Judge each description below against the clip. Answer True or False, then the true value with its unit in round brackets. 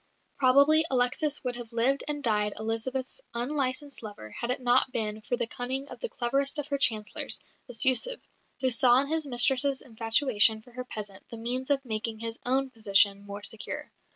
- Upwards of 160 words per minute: True (180 wpm)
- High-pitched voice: True (245 Hz)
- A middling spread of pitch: True (3.4 semitones)